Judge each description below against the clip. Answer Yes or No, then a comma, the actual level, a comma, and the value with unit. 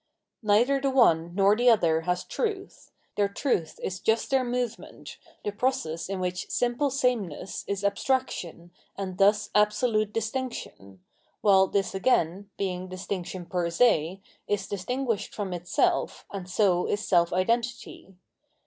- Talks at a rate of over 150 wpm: No, slow, 135 wpm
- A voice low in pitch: No, high, 200 Hz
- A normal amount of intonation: Yes, average, 4.7 semitones